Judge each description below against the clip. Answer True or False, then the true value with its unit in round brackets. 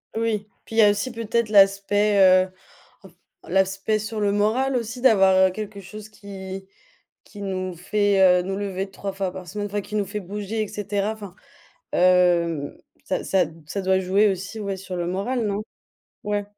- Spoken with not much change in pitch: True (1.9 semitones)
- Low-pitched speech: False (200 Hz)